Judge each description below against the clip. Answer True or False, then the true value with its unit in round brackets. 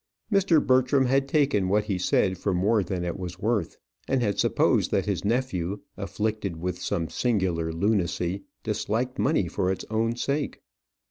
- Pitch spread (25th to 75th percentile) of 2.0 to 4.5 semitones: False (5.5 semitones)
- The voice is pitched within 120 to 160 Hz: False (105 Hz)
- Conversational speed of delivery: True (160 wpm)